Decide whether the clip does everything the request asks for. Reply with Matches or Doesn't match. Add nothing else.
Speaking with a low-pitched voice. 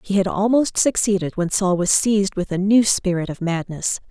Doesn't match